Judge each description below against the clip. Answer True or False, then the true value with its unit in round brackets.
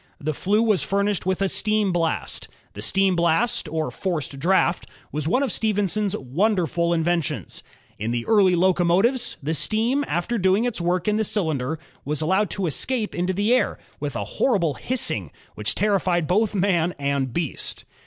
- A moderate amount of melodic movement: True (4.7 semitones)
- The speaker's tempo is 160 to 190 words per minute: True (165 wpm)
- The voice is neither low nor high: True (180 Hz)